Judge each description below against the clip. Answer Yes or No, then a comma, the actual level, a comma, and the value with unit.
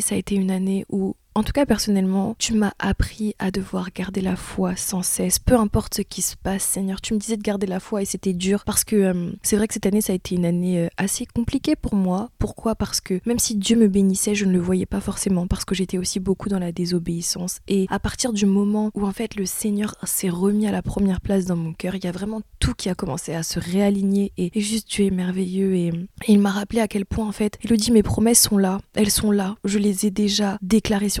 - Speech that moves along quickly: Yes, fast, 265 wpm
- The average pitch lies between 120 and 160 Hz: No, high, 200 Hz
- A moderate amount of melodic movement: No, narrow, 2.0 semitones